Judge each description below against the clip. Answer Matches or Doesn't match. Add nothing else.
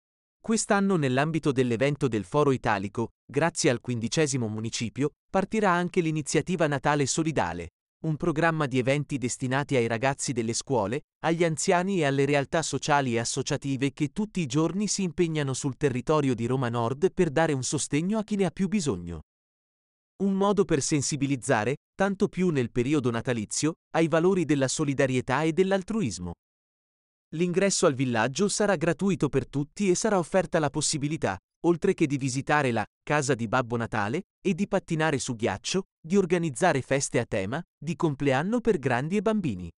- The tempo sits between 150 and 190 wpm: Matches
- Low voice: Doesn't match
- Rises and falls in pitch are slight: Doesn't match